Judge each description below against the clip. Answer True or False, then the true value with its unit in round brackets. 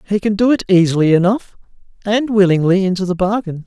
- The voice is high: True (195 Hz)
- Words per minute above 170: True (180 wpm)